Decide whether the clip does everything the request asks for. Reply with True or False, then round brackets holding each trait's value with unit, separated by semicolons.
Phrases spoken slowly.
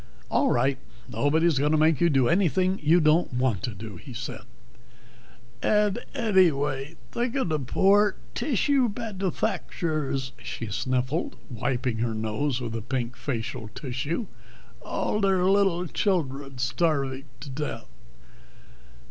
True (125 wpm)